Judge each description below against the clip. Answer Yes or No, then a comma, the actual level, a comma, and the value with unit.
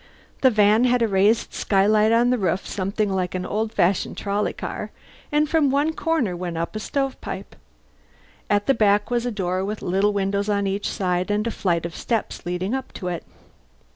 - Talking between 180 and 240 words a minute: Yes, average, 200 wpm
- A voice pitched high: Yes, high, 205 Hz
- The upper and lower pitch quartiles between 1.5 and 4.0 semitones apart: Yes, average, 3.5 semitones